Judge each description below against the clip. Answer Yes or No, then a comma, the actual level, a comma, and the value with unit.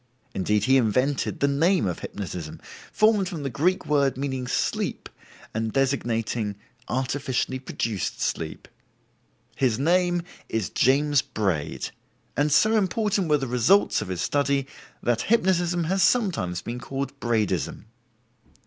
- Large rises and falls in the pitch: Yes, wide, 7.0 semitones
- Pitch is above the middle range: No, low, 135 Hz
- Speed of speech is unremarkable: No, slow, 130 wpm